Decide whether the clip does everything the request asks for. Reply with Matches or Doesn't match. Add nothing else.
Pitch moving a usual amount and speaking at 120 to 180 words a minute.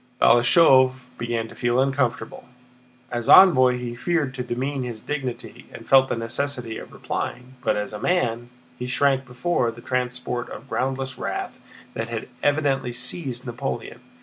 Doesn't match